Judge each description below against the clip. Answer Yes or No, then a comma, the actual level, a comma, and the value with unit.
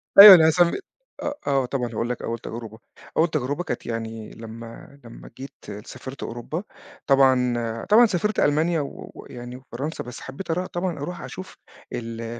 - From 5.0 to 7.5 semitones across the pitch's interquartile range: Yes, wide, 5.6 semitones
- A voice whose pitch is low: Yes, low, 130 Hz